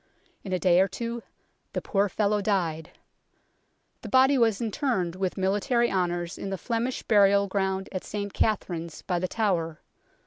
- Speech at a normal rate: Yes, average, 160 wpm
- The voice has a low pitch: No, high, 195 Hz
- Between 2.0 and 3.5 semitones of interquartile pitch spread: Yes, average, 3.2 semitones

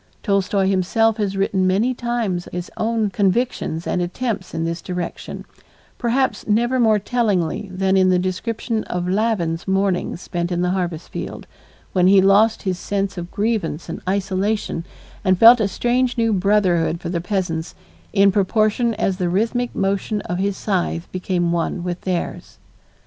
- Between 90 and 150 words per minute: No, average, 160 wpm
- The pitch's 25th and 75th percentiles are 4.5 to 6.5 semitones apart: No, average, 3.4 semitones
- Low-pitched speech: No, high, 195 Hz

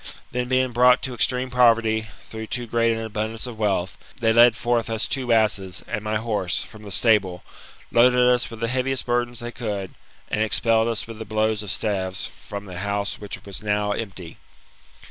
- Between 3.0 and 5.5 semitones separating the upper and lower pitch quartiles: No, narrow, 2.6 semitones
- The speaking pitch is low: Yes, low, 110 Hz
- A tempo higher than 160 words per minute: Yes, average, 195 wpm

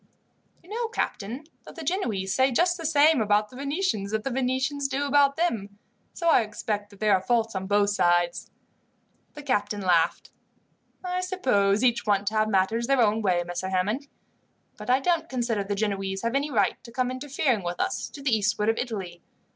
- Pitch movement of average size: No, wide, 5.7 semitones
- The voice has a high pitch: Yes, high, 225 Hz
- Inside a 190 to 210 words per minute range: Yes, average, 195 wpm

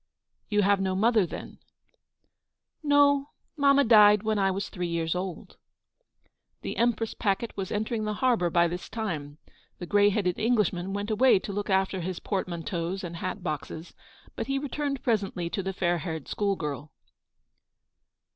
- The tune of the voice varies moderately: Yes, average, 3.9 semitones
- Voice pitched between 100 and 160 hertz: No, high, 195 Hz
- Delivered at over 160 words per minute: Yes, average, 170 wpm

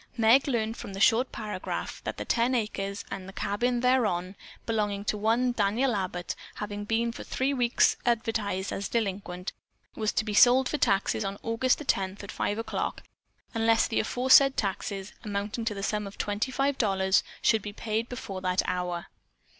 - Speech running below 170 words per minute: No, average, 175 wpm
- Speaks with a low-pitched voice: No, high, 215 Hz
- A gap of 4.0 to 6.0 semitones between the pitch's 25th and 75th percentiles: No, average, 3.1 semitones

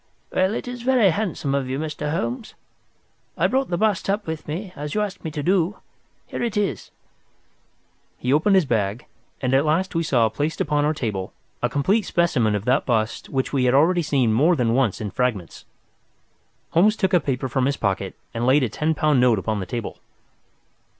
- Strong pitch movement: Yes, wide, 6.7 semitones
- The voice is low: No, medium, 145 Hz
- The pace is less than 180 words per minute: No, average, 200 wpm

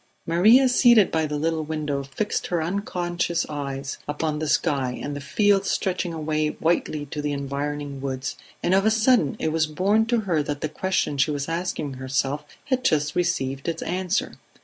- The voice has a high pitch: No, medium, 155 Hz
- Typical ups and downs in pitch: Yes, average, 4.2 semitones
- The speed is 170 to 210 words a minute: Yes, average, 180 wpm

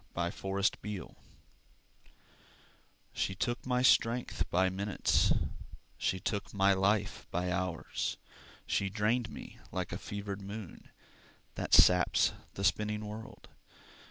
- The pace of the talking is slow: Yes, slow, 110 wpm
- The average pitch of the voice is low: Yes, low, 100 Hz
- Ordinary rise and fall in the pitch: No, narrow, 2.1 semitones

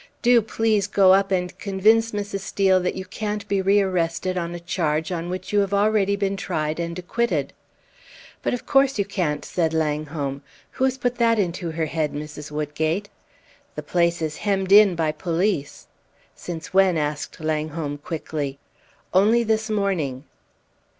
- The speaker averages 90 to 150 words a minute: No, average, 160 wpm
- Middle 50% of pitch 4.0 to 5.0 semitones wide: Yes, average, 4.3 semitones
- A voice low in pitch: No, medium, 185 Hz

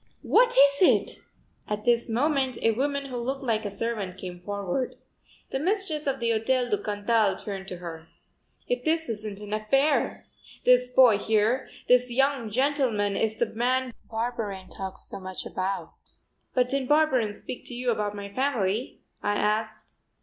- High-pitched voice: Yes, high, 230 Hz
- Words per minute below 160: No, average, 165 wpm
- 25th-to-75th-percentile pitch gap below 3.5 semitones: No, average, 4.2 semitones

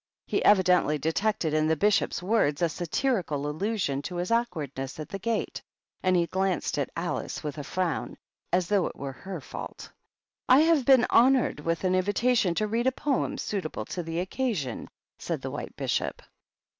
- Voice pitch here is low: No, medium, 185 Hz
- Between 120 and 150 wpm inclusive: No, average, 175 wpm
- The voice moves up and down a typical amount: No, wide, 5.9 semitones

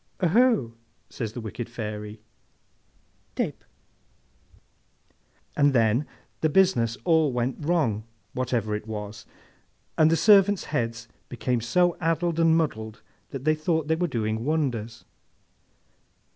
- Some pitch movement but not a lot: No, wide, 6.2 semitones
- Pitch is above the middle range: No, low, 130 Hz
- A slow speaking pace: Yes, slow, 115 wpm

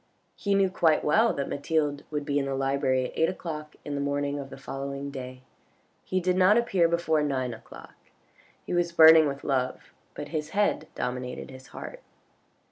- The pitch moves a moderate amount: Yes, average, 3.7 semitones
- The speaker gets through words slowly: No, average, 185 wpm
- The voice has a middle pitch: Yes, medium, 145 Hz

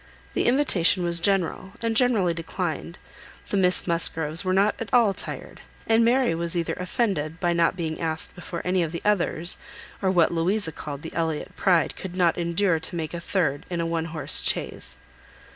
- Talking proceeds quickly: No, average, 185 wpm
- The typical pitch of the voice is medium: Yes, medium, 175 Hz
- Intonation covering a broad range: No, average, 2.8 semitones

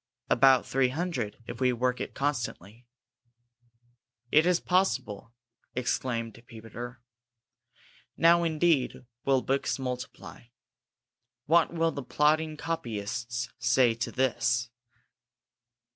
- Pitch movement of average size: Yes, average, 4.5 semitones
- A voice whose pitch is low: Yes, low, 130 Hz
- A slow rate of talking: Yes, slow, 100 wpm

